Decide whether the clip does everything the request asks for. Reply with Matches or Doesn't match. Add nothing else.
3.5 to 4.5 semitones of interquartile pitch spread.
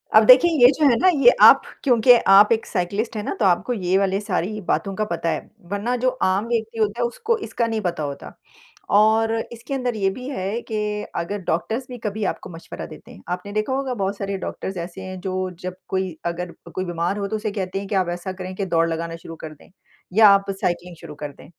Matches